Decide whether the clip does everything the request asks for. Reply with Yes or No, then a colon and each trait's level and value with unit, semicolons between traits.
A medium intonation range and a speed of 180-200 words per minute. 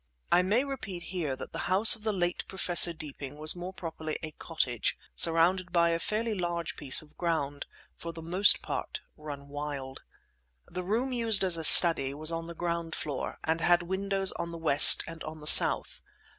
Yes: average, 3.1 semitones; average, 190 wpm